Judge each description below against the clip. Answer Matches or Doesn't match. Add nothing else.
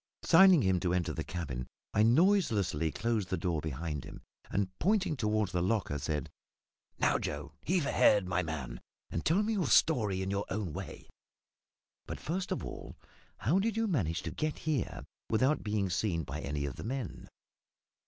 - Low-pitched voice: Matches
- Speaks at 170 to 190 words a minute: Matches